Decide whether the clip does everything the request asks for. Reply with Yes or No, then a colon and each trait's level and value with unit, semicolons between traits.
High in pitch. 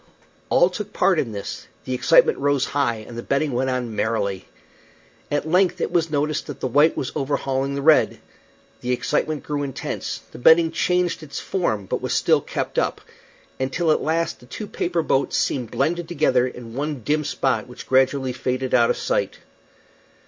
No: medium, 140 Hz